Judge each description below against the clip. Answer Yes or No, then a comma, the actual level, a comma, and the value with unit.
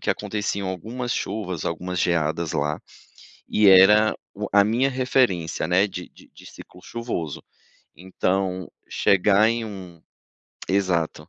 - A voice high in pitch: No, very low, 95 Hz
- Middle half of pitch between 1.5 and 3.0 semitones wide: No, average, 3.5 semitones